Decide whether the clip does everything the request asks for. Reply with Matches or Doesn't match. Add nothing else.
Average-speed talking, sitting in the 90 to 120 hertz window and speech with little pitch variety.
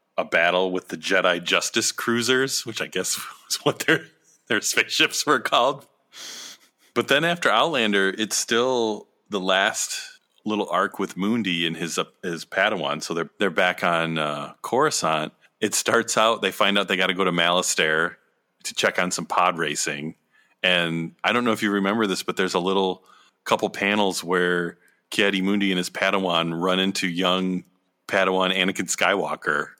Matches